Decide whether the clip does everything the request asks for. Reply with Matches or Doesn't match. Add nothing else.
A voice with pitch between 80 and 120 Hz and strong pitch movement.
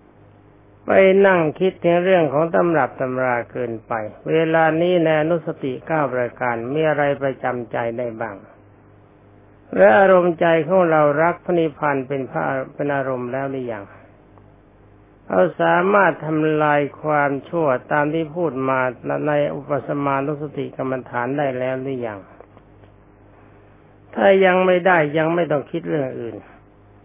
Doesn't match